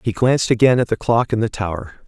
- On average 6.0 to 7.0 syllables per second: Yes, 6.4 syllables/s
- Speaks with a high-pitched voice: No, low, 110 Hz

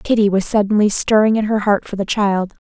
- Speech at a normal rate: No, fast, 225 wpm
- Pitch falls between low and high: No, high, 205 Hz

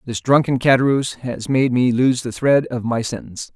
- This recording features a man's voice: Yes, male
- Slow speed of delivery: No, average, 200 wpm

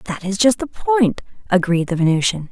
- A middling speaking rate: Yes, average, 190 wpm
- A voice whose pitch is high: Yes, high, 200 Hz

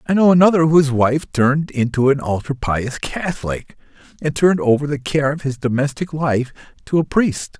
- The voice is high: No, medium, 145 Hz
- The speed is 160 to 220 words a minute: Yes, average, 180 wpm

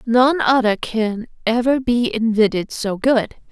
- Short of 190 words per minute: Yes, slow, 135 wpm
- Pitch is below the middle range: No, high, 230 Hz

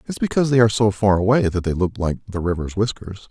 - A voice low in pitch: Yes, low, 105 Hz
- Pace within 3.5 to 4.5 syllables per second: No, 6.5 syllables/s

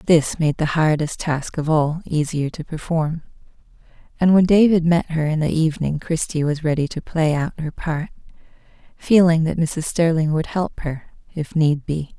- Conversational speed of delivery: Yes, average, 175 wpm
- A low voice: No, medium, 160 Hz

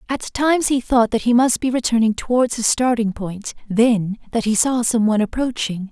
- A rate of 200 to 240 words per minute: Yes, fast, 205 wpm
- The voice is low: No, high, 230 Hz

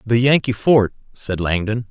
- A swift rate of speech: No, average, 155 wpm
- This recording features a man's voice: Yes, male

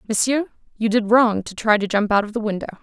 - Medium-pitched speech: No, high, 215 Hz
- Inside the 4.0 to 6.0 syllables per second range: No, 6.4 syllables/s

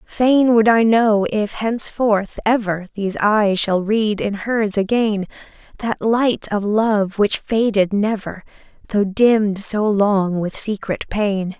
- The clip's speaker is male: No, female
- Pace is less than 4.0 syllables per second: Yes, 3.7 syllables/s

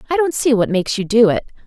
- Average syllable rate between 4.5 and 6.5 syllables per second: No, 7.3 syllables/s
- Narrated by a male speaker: No, female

